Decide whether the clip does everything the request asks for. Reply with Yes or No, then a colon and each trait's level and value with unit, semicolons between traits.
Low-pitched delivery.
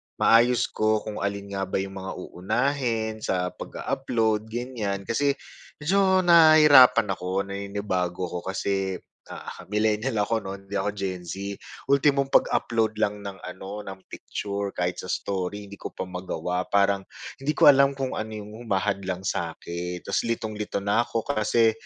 Yes: low, 105 Hz